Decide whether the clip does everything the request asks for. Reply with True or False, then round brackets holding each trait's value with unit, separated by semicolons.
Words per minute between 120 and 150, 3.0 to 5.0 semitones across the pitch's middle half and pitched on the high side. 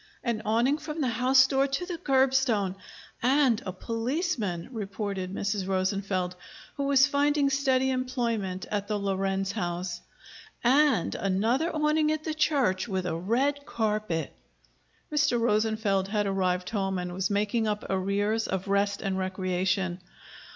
False (140 wpm; 5.6 semitones; 215 Hz)